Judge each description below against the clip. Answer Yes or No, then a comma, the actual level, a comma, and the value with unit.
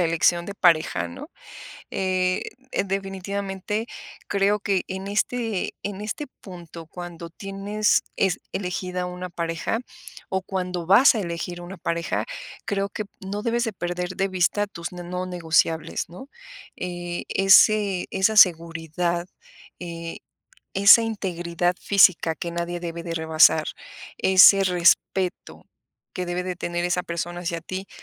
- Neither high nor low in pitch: Yes, medium, 180 Hz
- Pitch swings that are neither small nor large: No, narrow, 2.3 semitones